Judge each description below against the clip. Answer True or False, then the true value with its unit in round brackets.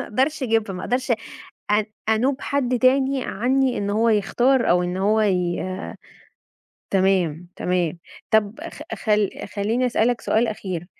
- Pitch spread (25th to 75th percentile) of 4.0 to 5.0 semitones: True (4.5 semitones)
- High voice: True (220 Hz)